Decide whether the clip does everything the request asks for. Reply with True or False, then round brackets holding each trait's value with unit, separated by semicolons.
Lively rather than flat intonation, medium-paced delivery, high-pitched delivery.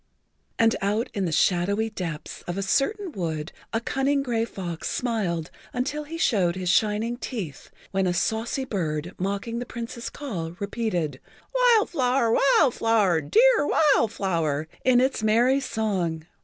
True (6.0 semitones; 155 wpm; 220 Hz)